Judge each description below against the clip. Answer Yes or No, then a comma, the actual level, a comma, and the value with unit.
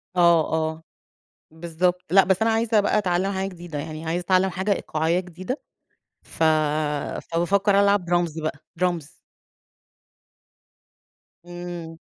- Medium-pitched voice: Yes, medium, 175 Hz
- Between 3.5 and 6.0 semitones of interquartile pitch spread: No, average, 2.7 semitones